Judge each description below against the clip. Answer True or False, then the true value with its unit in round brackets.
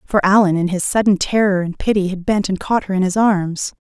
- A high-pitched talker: True (195 Hz)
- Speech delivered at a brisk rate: True (245 wpm)